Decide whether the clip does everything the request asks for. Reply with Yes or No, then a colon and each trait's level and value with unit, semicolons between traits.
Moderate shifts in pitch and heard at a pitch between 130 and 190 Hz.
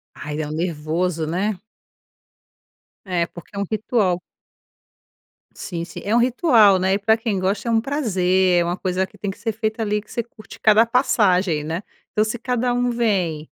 No: average, 4.1 semitones; high, 200 Hz